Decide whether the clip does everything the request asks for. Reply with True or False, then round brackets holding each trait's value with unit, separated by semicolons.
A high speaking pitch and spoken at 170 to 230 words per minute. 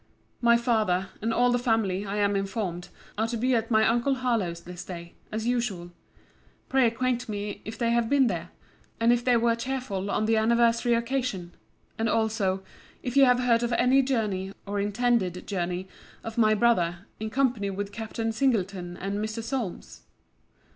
True (225 Hz; 175 wpm)